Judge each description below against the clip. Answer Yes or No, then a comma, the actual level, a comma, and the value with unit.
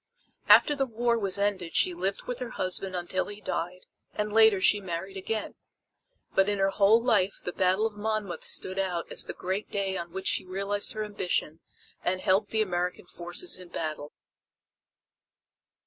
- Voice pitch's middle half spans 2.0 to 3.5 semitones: Yes, narrow, 2.5 semitones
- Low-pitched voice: No, high, 195 Hz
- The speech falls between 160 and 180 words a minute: Yes, average, 175 wpm